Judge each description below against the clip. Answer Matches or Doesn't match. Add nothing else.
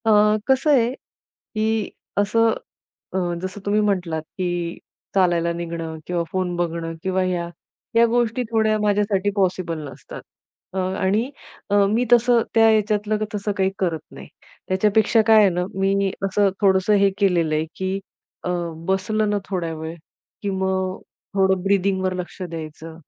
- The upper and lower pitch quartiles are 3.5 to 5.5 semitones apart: Doesn't match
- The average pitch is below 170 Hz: Doesn't match